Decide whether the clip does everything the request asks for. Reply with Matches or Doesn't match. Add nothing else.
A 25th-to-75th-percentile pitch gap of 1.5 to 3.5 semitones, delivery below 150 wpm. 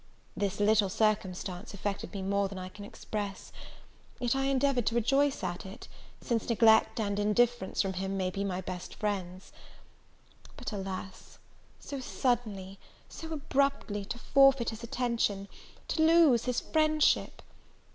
Doesn't match